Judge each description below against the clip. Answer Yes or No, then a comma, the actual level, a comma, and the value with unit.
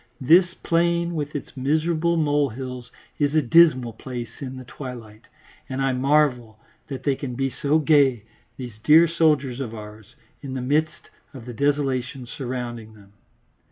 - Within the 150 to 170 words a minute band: Yes, average, 155 wpm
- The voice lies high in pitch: No, low, 135 Hz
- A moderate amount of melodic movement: Yes, average, 3.6 semitones